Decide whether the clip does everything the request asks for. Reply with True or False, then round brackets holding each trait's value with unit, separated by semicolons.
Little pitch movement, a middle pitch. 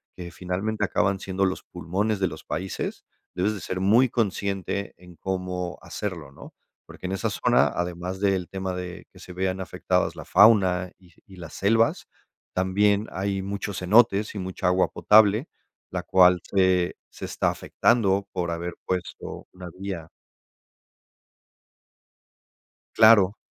False (1.9 semitones; 95 Hz)